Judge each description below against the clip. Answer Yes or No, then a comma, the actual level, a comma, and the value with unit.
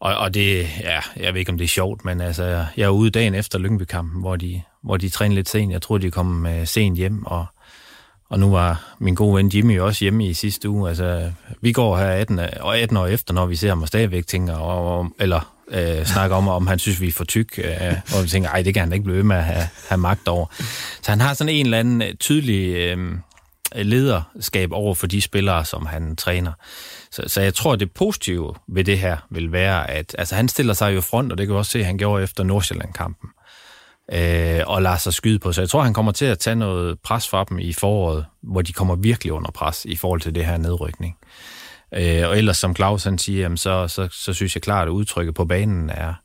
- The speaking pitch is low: Yes, very low, 95 Hz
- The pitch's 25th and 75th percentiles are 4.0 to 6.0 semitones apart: No, average, 3.0 semitones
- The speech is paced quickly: Yes, fast, 240 wpm